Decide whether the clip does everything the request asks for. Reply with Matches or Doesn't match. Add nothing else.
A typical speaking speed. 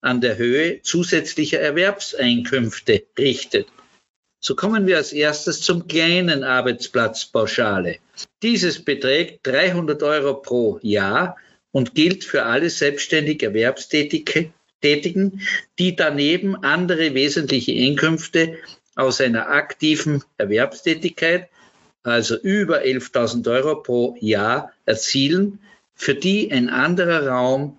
Doesn't match